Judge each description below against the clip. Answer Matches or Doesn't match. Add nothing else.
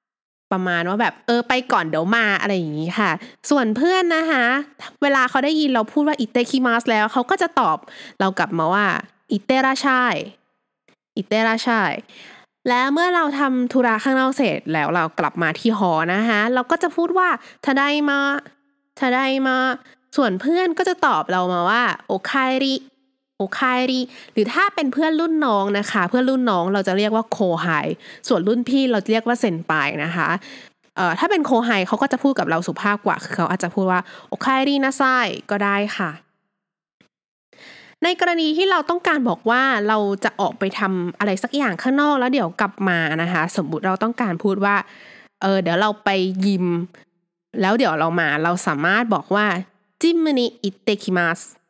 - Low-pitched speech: Doesn't match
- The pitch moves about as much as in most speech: Doesn't match